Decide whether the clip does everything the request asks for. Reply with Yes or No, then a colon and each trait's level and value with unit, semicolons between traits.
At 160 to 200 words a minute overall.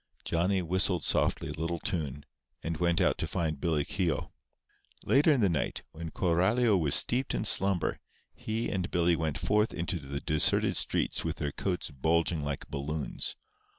Yes: average, 165 wpm